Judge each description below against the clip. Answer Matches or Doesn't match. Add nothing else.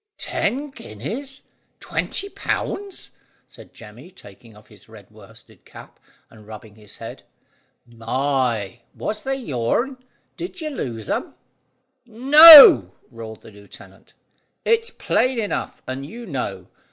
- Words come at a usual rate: Doesn't match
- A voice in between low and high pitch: Doesn't match